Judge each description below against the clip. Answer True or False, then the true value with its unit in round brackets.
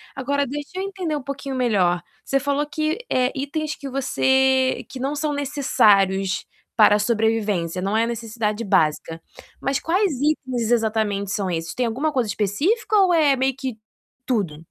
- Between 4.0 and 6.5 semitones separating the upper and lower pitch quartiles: True (5.2 semitones)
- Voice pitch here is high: True (255 Hz)